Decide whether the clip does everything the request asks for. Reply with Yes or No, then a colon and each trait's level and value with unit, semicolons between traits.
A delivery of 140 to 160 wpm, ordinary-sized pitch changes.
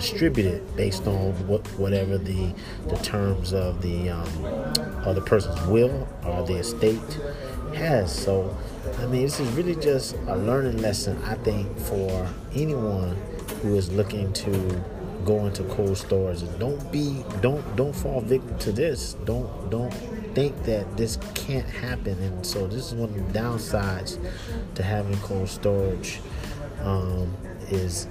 Yes: average, 145 wpm; average, 3.8 semitones